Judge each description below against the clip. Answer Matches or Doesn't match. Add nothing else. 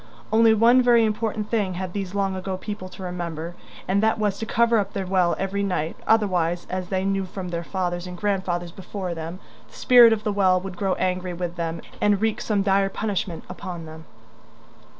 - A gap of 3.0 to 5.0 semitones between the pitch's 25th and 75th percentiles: Doesn't match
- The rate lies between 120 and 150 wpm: Doesn't match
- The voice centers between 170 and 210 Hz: Matches